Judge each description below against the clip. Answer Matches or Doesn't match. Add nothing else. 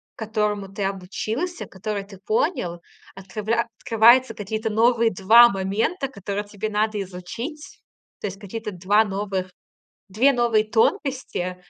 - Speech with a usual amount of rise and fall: Matches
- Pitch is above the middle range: Matches